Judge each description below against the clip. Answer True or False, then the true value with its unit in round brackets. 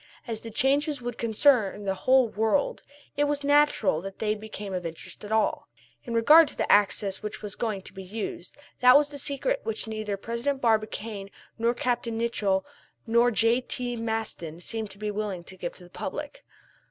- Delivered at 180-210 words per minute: True (190 wpm)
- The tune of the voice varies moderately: True (3.7 semitones)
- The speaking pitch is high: True (225 Hz)